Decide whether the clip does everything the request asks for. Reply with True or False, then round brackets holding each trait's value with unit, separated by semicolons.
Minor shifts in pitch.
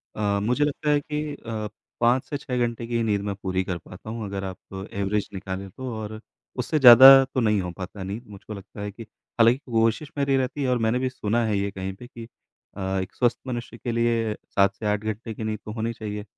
False (3.4 semitones)